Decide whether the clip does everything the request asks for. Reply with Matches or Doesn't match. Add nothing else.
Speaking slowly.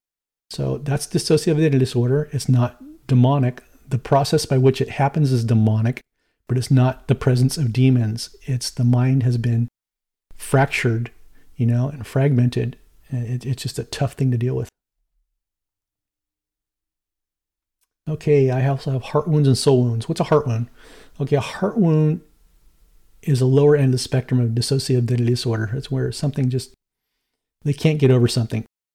Doesn't match